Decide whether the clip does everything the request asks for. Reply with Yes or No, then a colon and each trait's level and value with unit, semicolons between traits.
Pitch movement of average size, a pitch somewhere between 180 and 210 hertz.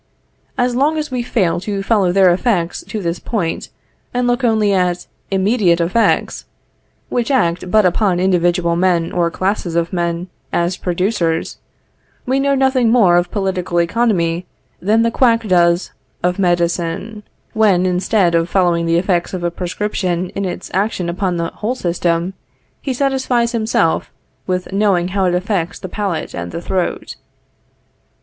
Yes: average, 4.1 semitones; medium, 185 Hz